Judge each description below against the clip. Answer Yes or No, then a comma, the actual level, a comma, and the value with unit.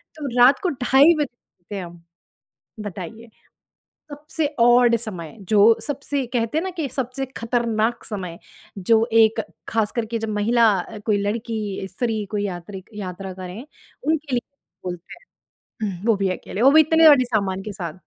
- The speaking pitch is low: No, high, 225 Hz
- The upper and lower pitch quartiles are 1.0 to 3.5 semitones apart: No, average, 4.3 semitones